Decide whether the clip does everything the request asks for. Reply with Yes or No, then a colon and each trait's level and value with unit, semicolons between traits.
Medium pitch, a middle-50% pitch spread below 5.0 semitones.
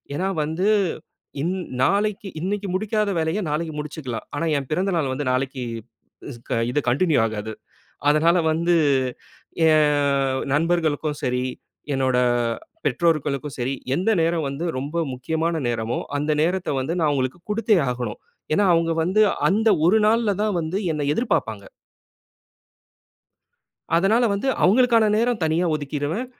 No: medium, 160 Hz; wide, 5.6 semitones